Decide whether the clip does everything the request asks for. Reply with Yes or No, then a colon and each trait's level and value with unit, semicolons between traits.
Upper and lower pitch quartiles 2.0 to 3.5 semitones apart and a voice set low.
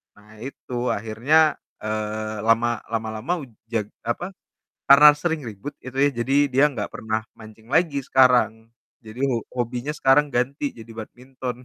No: average, 4.0 semitones; low, 120 Hz